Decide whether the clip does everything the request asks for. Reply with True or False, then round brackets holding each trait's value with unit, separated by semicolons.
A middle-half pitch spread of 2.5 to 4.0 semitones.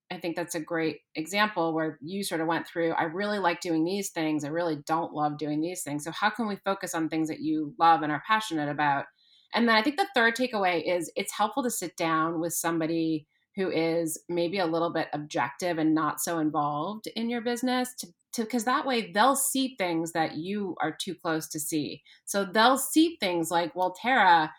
False (4.6 semitones)